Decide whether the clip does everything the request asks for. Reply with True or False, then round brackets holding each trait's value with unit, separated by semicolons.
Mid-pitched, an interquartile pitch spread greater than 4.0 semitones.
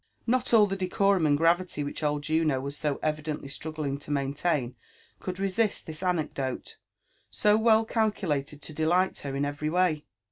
True (155 Hz; 4.5 semitones)